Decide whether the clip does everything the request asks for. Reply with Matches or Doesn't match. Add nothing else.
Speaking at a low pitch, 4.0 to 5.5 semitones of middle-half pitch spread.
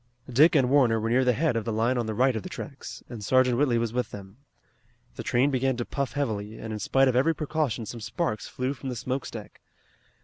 Doesn't match